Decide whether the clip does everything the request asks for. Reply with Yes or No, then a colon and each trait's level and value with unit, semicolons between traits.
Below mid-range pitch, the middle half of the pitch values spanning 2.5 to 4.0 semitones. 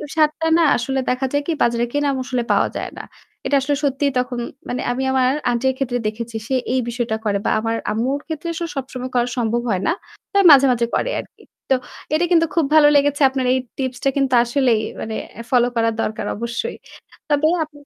No: very high, 260 Hz; average, 3.2 semitones